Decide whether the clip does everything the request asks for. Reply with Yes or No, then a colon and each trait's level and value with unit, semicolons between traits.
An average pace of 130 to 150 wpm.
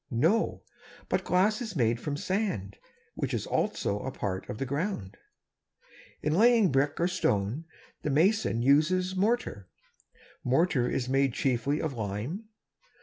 Yes: average, 140 wpm